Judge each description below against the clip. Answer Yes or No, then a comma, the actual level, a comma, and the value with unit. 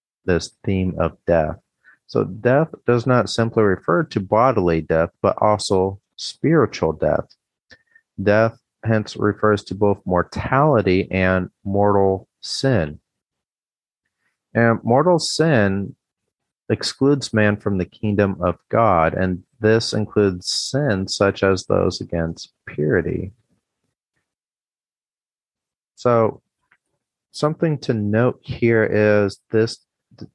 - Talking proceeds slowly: Yes, slow, 105 wpm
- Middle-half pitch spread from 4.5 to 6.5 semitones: No, average, 4.1 semitones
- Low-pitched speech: Yes, low, 105 Hz